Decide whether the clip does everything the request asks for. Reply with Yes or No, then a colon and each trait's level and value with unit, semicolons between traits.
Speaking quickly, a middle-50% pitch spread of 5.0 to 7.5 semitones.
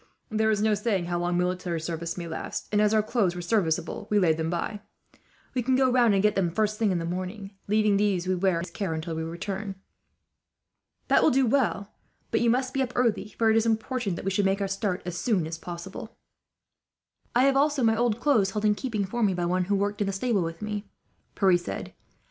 No: fast, 235 wpm; average, 3.9 semitones